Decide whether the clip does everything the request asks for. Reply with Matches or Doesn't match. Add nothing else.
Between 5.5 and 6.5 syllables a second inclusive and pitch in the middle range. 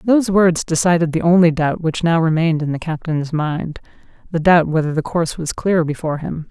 Matches